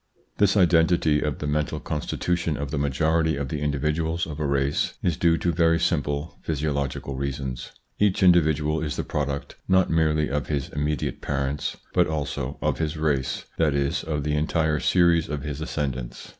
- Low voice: Yes, very low, 75 Hz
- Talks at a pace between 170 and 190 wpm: Yes, average, 175 wpm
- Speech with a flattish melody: Yes, narrow, 2.3 semitones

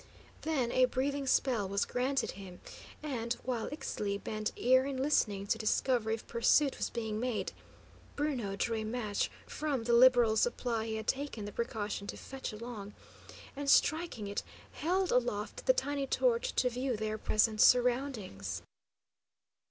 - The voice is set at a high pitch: Yes, high, 240 Hz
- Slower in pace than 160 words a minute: Yes, average, 150 wpm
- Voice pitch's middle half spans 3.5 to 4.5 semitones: Yes, average, 4.1 semitones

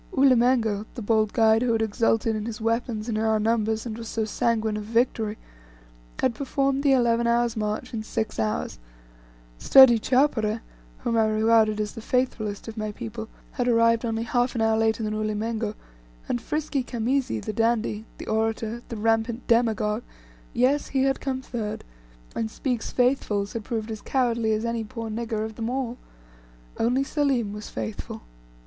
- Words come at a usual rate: Yes, average, 170 wpm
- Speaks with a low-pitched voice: No, high, 225 Hz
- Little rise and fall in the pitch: Yes, narrow, 1.9 semitones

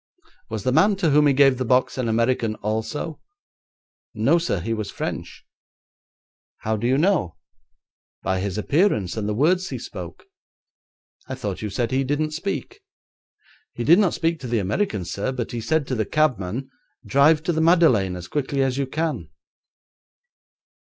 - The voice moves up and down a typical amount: No, wide, 6.2 semitones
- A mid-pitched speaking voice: No, low, 130 Hz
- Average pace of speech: Yes, average, 170 wpm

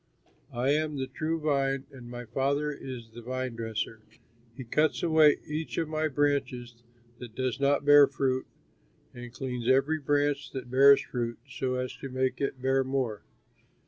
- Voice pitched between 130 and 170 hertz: Yes, low, 135 Hz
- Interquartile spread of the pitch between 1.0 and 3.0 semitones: Yes, narrow, 2.6 semitones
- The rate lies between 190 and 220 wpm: No, average, 165 wpm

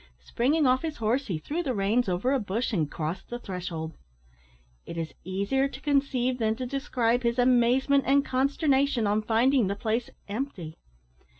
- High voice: Yes, high, 245 Hz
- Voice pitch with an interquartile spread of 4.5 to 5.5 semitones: Yes, average, 5.1 semitones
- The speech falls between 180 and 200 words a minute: No, average, 170 wpm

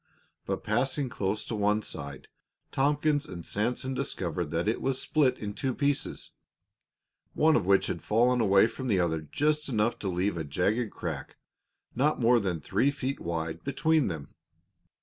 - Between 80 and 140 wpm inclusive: No, average, 165 wpm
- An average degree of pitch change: No, wide, 6.8 semitones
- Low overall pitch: Yes, low, 110 Hz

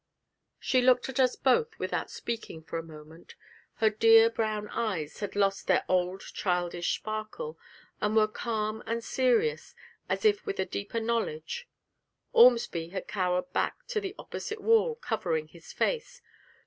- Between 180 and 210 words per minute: No, average, 150 wpm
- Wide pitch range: Yes, wide, 6.1 semitones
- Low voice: No, high, 220 Hz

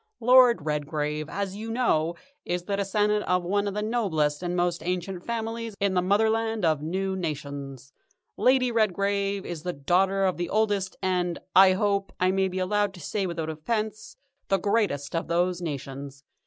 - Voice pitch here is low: No, medium, 185 Hz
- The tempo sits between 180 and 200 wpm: No, average, 170 wpm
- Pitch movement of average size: Yes, average, 3.7 semitones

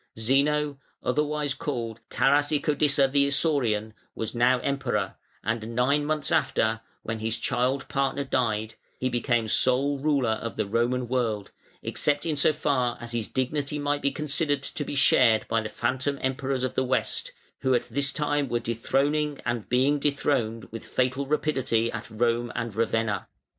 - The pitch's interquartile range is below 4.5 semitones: Yes, average, 3.7 semitones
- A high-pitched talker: No, low, 130 Hz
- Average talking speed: Yes, average, 160 wpm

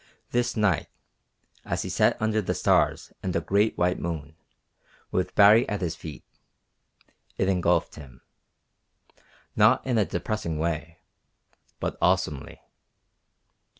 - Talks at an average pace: No, slow, 120 wpm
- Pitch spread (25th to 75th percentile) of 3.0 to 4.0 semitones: No, average, 4.4 semitones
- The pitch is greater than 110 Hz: No, very low, 90 Hz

